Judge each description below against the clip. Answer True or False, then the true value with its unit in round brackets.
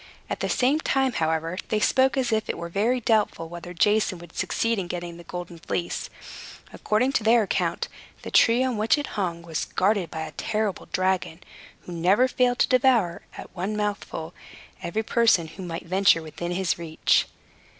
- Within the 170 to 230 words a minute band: True (180 wpm)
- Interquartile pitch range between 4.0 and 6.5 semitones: True (4.9 semitones)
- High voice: True (195 Hz)